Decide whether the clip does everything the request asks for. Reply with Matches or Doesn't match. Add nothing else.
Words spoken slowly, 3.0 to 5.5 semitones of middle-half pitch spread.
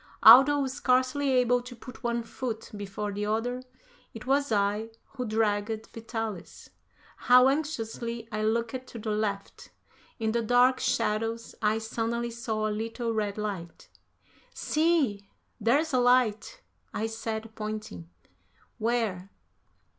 Doesn't match